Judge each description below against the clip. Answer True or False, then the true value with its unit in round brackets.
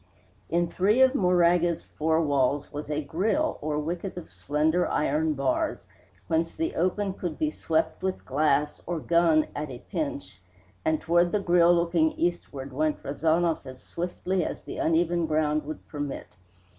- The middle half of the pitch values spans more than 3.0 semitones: False (2.6 semitones)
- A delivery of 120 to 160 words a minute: True (155 wpm)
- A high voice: False (160 Hz)